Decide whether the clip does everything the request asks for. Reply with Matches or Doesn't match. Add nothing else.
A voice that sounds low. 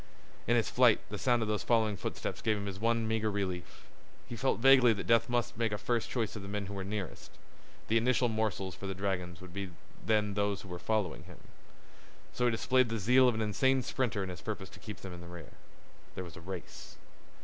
Matches